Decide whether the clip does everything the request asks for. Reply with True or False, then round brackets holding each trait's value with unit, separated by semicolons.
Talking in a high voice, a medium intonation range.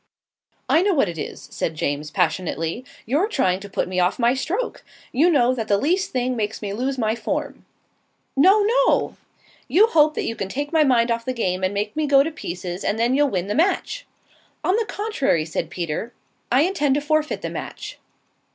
False (255 Hz; 7.7 semitones)